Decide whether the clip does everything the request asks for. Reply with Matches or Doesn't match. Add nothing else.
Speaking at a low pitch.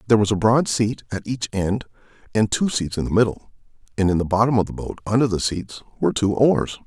Matches